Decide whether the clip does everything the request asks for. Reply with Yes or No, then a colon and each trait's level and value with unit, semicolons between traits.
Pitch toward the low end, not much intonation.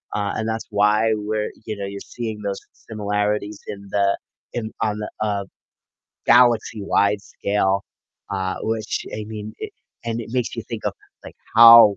Yes: low, 105 Hz; narrow, 1.6 semitones